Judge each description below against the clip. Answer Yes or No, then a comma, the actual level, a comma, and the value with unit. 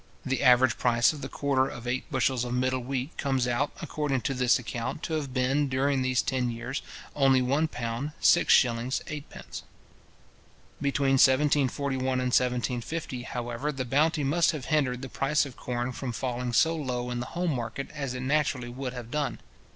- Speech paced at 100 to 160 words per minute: No, average, 170 wpm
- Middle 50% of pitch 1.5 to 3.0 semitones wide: Yes, narrow, 2.4 semitones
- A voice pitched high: No, low, 130 Hz